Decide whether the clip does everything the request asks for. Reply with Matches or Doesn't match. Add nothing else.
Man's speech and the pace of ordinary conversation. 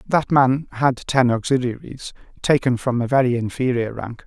Matches